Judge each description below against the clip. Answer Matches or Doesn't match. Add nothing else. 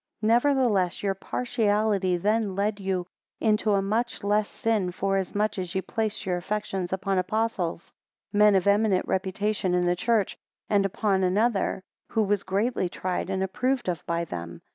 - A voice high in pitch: Matches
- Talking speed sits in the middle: Matches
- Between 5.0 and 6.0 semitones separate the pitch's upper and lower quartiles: Doesn't match